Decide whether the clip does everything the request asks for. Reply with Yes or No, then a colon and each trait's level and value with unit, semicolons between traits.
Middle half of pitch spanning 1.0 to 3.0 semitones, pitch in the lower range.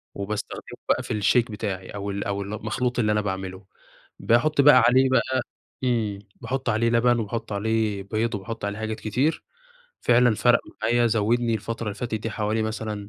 Yes: narrow, 2.6 semitones; low, 110 Hz